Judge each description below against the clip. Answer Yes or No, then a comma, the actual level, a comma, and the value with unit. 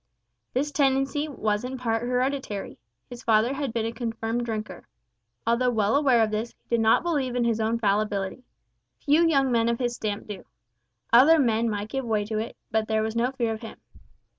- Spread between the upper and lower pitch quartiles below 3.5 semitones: Yes, average, 3.0 semitones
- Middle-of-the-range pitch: No, high, 235 Hz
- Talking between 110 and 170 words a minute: No, average, 195 wpm